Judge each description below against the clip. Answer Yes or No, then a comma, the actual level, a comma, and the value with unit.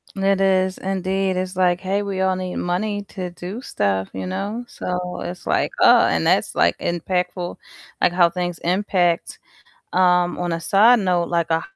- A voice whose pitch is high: No, medium, 180 Hz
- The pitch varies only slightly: Yes, narrow, 1.6 semitones